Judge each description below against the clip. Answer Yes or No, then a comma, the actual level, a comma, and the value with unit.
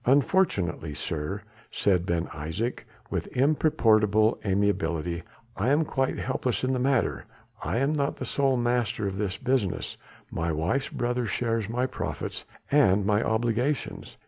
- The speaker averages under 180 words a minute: Yes, average, 140 wpm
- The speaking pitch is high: No, low, 115 Hz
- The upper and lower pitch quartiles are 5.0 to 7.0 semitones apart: Yes, wide, 5.4 semitones